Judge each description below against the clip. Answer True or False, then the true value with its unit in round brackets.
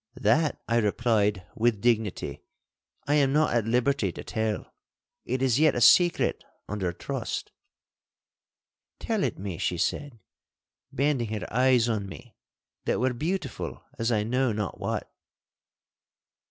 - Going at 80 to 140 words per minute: True (135 wpm)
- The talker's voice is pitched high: False (120 Hz)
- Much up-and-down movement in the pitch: False (4.0 semitones)